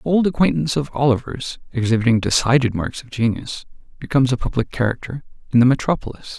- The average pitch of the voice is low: Yes, low, 130 Hz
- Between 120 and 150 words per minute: No, average, 160 wpm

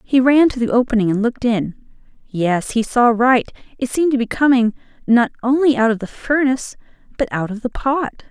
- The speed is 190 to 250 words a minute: Yes, average, 200 wpm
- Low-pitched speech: No, high, 240 Hz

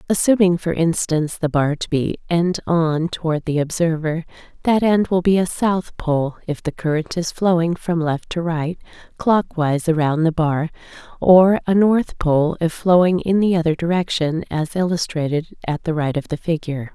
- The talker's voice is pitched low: No, medium, 165 Hz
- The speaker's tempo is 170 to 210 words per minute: Yes, average, 175 wpm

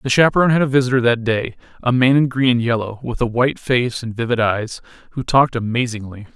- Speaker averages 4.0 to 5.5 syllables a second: No, 6.3 syllables/s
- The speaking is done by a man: Yes, male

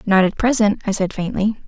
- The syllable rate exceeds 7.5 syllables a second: No, 5.5 syllables/s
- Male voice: No, female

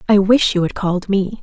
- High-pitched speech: Yes, high, 195 Hz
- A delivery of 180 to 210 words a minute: No, fast, 255 wpm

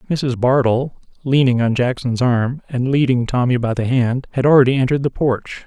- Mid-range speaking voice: No, low, 125 Hz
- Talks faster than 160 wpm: Yes, average, 180 wpm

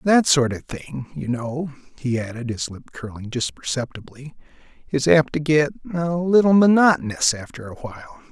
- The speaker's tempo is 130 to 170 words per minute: Yes, average, 165 wpm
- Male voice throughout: Yes, male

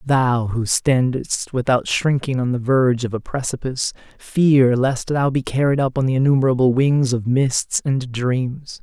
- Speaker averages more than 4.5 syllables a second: No, 4.4 syllables/s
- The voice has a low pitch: Yes, low, 130 Hz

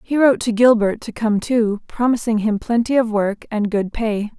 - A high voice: Yes, high, 225 Hz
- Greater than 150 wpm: Yes, fast, 205 wpm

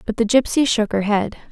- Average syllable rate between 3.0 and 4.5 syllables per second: No, 5.7 syllables/s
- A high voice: Yes, high, 225 Hz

